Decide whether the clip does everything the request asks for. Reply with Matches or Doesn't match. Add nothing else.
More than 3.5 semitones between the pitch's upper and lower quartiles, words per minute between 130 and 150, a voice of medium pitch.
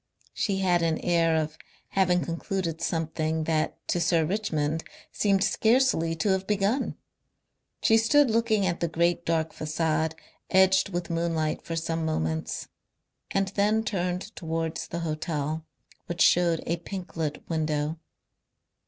Doesn't match